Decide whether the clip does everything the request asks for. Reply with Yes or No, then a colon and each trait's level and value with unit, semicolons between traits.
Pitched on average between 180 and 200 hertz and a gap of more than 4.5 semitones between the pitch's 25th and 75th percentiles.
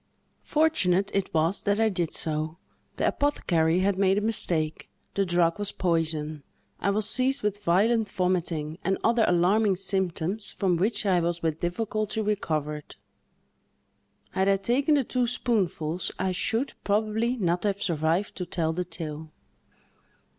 No: high, 190 Hz; average, 4.1 semitones